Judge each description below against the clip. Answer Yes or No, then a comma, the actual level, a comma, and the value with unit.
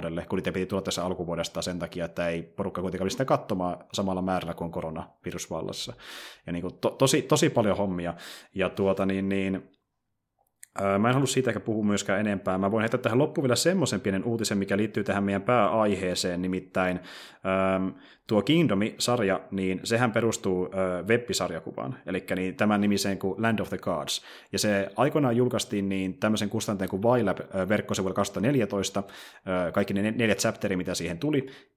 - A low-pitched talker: Yes, low, 100 Hz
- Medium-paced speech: No, fast, 160 wpm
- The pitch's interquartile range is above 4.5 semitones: No, average, 2.8 semitones